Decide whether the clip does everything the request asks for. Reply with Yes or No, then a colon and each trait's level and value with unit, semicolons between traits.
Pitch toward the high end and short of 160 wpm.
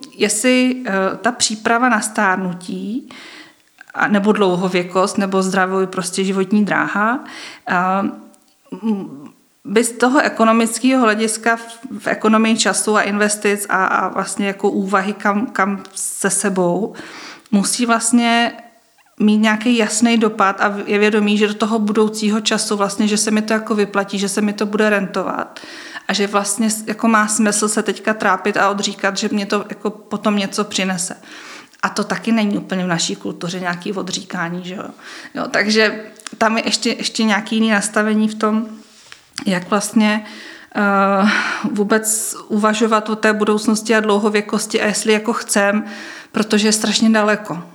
Yes: high, 215 Hz; average, 145 wpm